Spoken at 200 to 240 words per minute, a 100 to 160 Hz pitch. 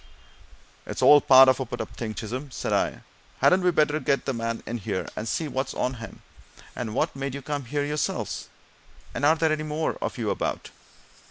Yes: fast, 205 wpm; low, 135 Hz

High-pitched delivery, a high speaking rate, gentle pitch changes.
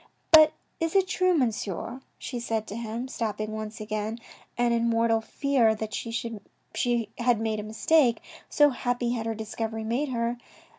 No: high, 230 Hz; average, 165 wpm; narrow, 2.1 semitones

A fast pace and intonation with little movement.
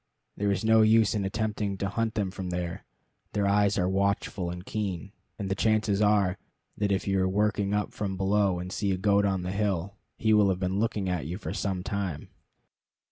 Yes: fast, 210 wpm; narrow, 1.8 semitones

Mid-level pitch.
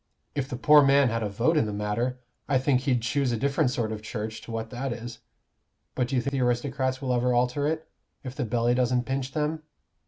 No: low, 125 Hz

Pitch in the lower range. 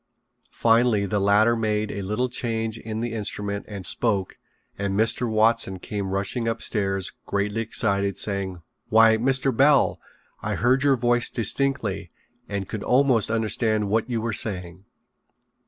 Yes: low, 110 Hz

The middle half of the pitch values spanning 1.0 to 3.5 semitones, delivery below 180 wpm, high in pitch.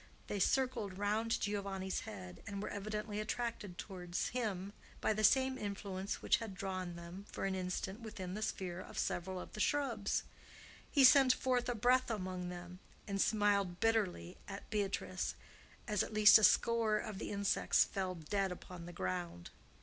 Yes: average, 2.9 semitones; average, 165 wpm; high, 200 Hz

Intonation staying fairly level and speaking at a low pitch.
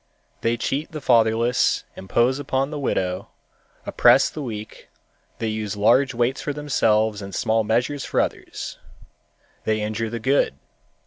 No: average, 3.7 semitones; low, 115 Hz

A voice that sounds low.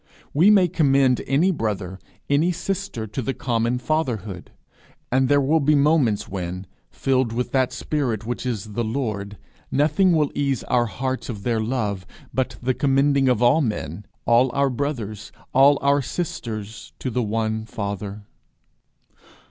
Yes: low, 125 Hz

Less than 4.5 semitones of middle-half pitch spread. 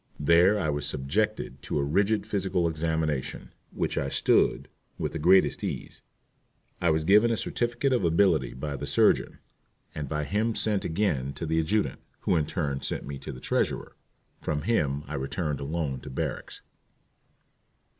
No: average, 5.3 semitones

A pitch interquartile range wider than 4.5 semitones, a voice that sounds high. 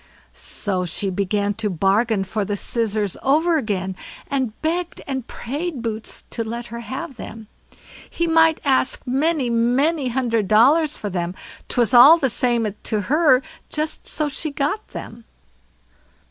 Yes: wide, 5.6 semitones; high, 240 Hz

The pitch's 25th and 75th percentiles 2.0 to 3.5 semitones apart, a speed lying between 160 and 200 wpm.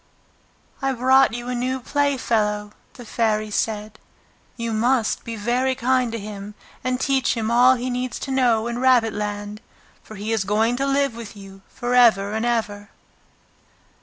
Yes: average, 3.0 semitones; average, 165 wpm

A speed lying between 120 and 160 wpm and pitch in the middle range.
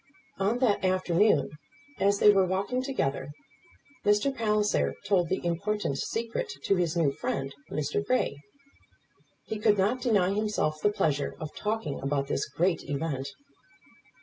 No: average, 140 wpm; high, 195 Hz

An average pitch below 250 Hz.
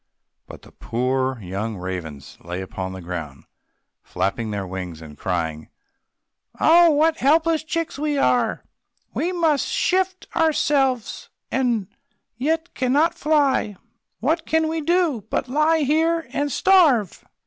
No: very high, 265 Hz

